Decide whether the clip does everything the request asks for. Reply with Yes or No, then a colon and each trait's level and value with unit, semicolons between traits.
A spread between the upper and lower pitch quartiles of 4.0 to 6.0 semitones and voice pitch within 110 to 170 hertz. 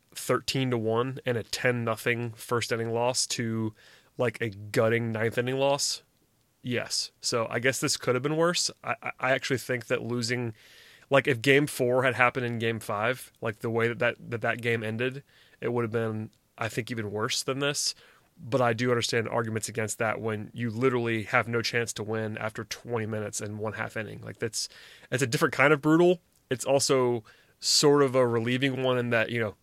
No: average, 2.7 semitones; low, 120 Hz